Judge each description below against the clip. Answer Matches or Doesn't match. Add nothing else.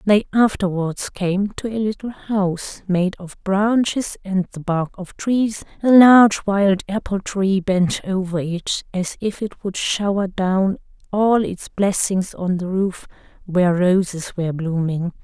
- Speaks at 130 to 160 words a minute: Matches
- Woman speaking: Matches